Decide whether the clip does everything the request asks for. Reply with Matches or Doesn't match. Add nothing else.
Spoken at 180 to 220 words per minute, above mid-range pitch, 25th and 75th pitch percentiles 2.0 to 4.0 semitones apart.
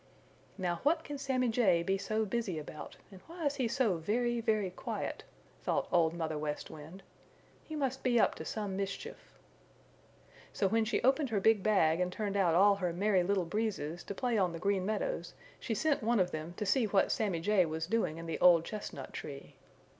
Doesn't match